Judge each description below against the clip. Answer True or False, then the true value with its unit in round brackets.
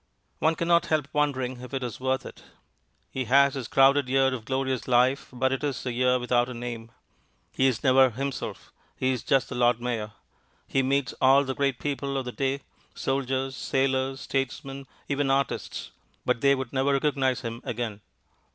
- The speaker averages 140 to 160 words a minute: False (180 wpm)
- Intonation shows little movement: True (1.7 semitones)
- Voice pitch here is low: True (130 Hz)